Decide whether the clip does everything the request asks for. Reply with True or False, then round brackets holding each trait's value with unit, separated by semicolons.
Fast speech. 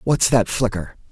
False (160 wpm)